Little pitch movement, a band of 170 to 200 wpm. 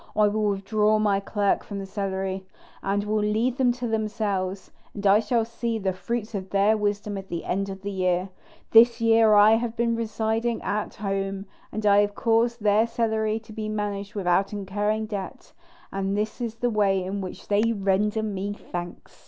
Yes: narrow, 2.1 semitones; average, 185 wpm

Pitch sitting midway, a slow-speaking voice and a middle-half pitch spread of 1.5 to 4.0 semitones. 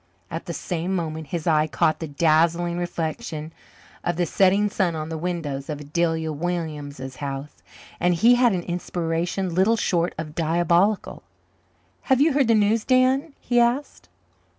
No: medium, 170 Hz; average, 155 wpm; average, 3.7 semitones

